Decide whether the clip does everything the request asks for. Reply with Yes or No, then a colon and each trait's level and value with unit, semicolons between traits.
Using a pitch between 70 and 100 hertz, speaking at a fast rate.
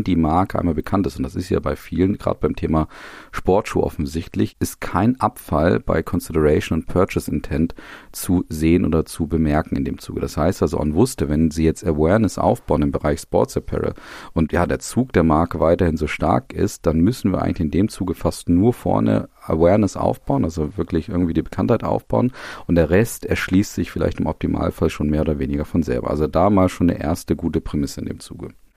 Yes: very low, 85 Hz; fast, 205 wpm